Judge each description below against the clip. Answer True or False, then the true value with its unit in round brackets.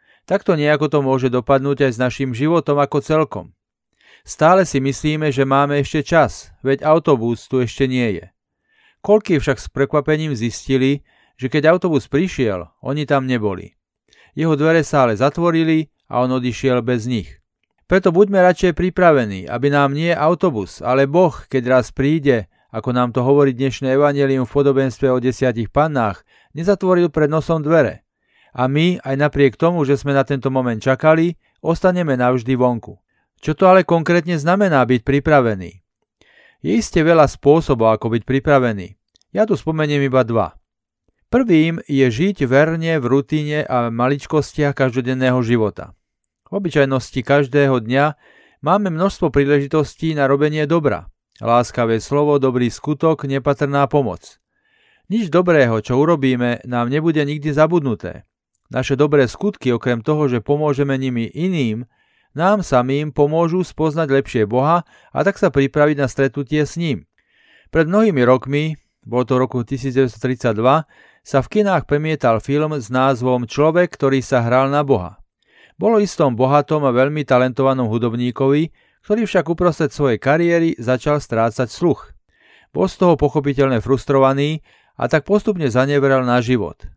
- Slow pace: False (145 wpm)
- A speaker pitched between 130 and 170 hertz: True (140 Hz)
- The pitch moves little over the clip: False (3.7 semitones)